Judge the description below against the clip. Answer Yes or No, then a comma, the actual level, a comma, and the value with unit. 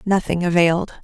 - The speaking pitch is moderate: Yes, medium, 175 Hz